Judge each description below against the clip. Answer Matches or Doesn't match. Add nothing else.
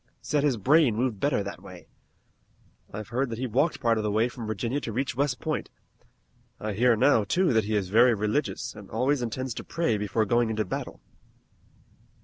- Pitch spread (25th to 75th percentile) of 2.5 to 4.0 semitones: Matches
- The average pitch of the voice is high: Doesn't match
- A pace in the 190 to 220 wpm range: Matches